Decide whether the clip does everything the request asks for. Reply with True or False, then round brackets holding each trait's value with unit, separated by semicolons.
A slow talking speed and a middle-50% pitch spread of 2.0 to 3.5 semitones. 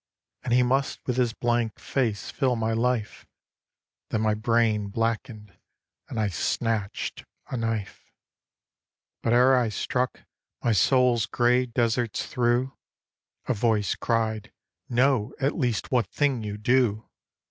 True (130 wpm; 2.5 semitones)